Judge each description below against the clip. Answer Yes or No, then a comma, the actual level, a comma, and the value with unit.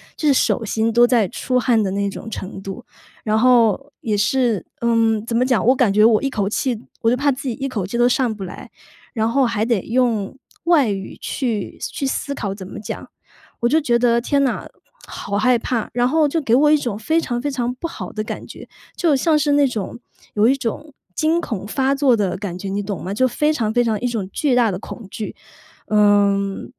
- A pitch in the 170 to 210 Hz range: No, high, 235 Hz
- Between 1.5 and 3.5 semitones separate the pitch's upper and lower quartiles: No, average, 4.0 semitones